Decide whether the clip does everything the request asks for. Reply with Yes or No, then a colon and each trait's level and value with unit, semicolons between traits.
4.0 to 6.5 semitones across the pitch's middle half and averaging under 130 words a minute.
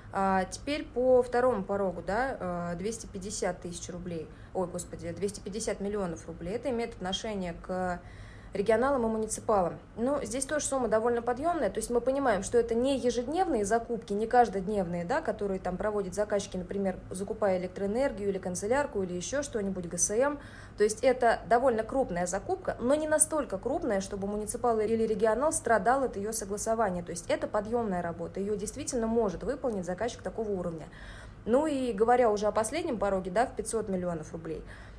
No: average, 4.5 semitones; fast, 160 wpm